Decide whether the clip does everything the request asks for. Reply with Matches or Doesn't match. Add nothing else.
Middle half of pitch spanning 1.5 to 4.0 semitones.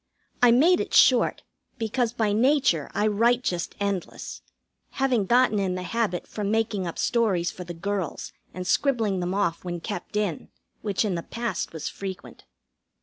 Doesn't match